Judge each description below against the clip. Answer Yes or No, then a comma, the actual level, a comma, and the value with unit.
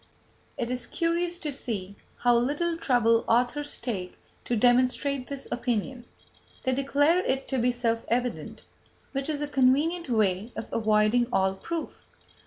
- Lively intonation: No, average, 3.8 semitones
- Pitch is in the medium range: No, very high, 250 Hz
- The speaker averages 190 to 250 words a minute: No, average, 145 wpm